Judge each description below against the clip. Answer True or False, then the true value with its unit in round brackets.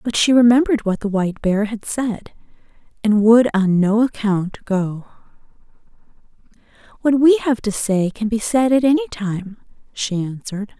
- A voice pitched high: True (220 Hz)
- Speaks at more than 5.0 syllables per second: False (4.8 syllables/s)